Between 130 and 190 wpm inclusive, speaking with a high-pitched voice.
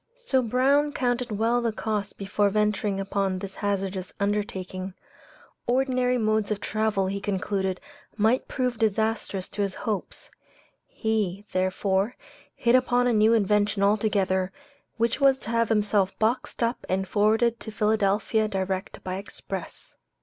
Yes: slow, 135 wpm; high, 210 Hz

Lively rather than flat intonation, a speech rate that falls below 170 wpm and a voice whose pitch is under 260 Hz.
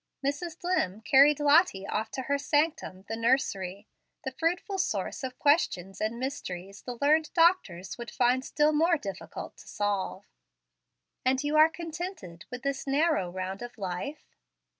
No: wide, 7.5 semitones; average, 150 wpm; very high, 265 Hz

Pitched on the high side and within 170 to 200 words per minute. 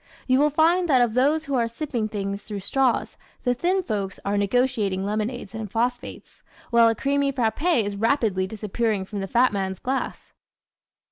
Yes: high, 230 Hz; average, 175 wpm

